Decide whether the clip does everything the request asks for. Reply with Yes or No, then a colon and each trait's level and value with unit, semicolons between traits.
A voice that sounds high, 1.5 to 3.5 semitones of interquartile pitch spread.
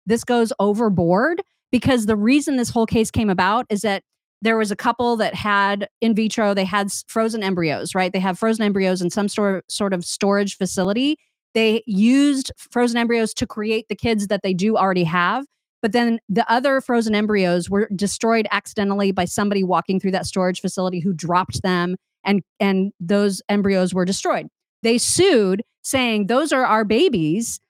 Yes: high, 205 Hz; average, 3.2 semitones